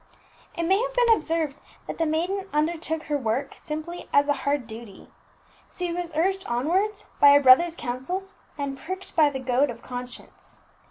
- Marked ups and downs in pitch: No, average, 4.9 semitones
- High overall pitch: Yes, very high, 310 Hz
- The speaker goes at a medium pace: Yes, average, 170 wpm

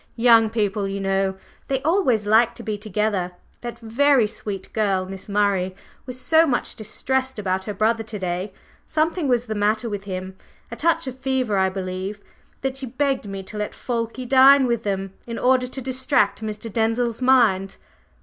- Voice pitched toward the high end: Yes, high, 220 Hz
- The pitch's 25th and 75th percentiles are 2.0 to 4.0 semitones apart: No, average, 4.5 semitones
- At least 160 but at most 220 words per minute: Yes, average, 180 wpm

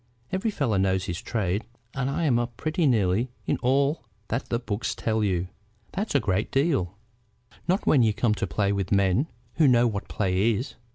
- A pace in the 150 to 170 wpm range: No, average, 185 wpm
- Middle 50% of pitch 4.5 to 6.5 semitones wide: Yes, wide, 5.5 semitones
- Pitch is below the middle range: Yes, low, 115 Hz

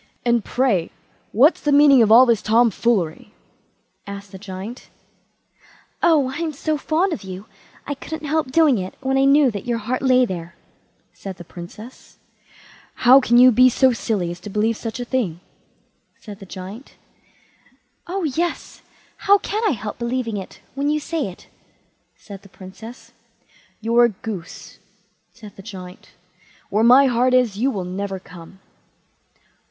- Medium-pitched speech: No, high, 235 Hz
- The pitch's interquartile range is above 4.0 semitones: Yes, average, 5.3 semitones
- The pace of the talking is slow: No, average, 160 wpm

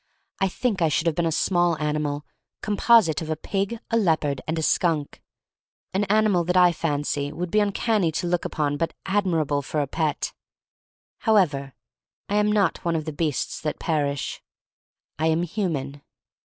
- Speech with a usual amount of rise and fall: Yes, average, 4.3 semitones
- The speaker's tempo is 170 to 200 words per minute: Yes, average, 175 wpm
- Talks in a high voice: No, medium, 165 Hz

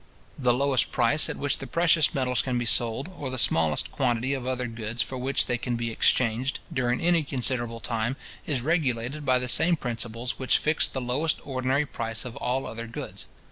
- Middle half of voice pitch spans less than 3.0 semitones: Yes, narrow, 2.6 semitones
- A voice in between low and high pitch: No, low, 125 Hz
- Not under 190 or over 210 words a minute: Yes, average, 195 wpm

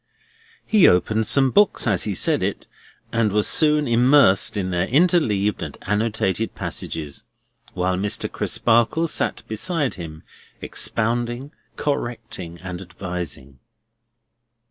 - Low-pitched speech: Yes, low, 110 Hz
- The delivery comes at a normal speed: No, slow, 115 wpm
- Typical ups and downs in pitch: No, wide, 5.9 semitones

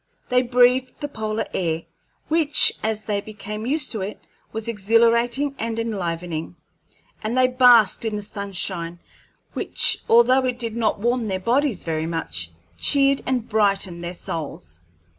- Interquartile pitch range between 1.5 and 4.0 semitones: No, average, 4.7 semitones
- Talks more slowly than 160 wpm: Yes, average, 145 wpm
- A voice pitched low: No, high, 220 Hz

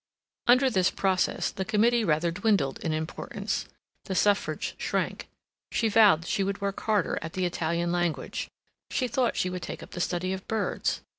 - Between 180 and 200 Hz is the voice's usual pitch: Yes, high, 190 Hz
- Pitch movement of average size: Yes, average, 3.6 semitones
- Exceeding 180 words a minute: No, average, 170 wpm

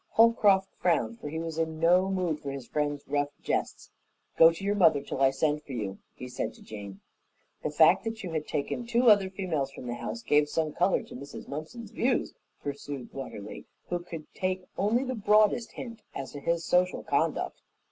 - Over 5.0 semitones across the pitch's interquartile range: Yes, wide, 5.5 semitones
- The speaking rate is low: No, average, 200 wpm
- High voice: No, medium, 160 Hz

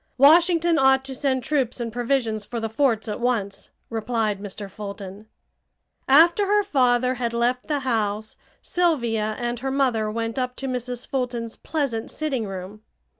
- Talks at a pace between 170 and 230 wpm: No, average, 155 wpm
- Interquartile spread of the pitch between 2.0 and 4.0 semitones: Yes, average, 3.5 semitones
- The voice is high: Yes, high, 245 Hz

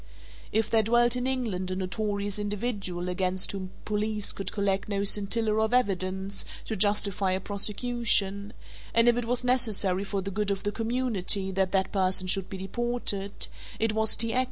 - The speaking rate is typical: Yes, average, 180 wpm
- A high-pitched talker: Yes, high, 205 Hz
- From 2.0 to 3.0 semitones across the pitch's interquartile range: Yes, average, 2.7 semitones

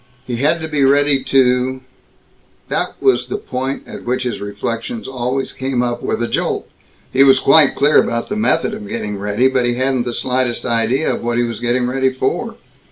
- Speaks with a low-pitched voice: Yes, low, 130 Hz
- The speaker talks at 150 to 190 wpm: No, average, 200 wpm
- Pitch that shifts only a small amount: Yes, narrow, 2.2 semitones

